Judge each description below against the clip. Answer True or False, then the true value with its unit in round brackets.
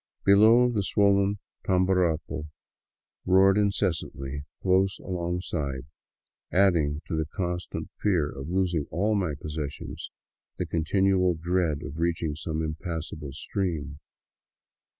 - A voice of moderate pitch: False (85 Hz)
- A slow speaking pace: True (110 wpm)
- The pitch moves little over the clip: False (3.7 semitones)